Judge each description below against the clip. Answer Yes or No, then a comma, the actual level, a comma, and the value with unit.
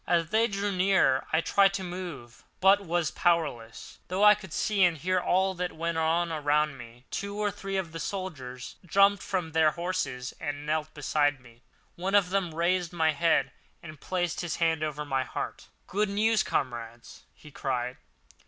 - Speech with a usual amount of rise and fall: Yes, average, 4.4 semitones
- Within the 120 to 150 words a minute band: No, average, 180 wpm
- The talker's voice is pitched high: No, medium, 170 Hz